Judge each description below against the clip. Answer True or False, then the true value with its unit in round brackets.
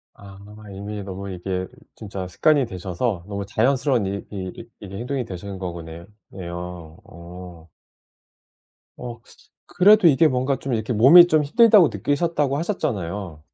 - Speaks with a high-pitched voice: False (100 Hz)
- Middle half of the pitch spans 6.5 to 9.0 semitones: True (6.9 semitones)